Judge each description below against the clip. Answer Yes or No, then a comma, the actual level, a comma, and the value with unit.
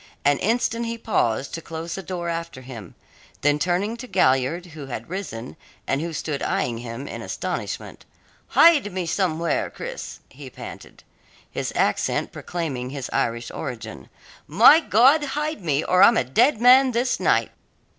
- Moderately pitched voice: Yes, medium, 170 Hz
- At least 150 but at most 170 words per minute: Yes, average, 155 wpm